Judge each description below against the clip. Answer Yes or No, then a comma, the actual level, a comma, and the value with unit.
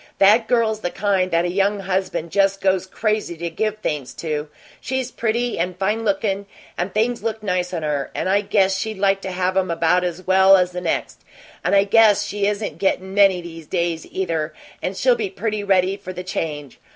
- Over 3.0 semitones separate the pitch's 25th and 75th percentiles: No, narrow, 2.6 semitones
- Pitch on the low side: No, high, 190 Hz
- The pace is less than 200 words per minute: No, fast, 205 wpm